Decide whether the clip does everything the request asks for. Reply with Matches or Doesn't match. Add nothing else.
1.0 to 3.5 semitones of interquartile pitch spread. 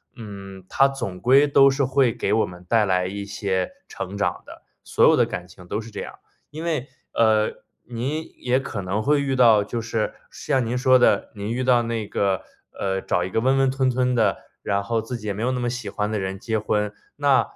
Doesn't match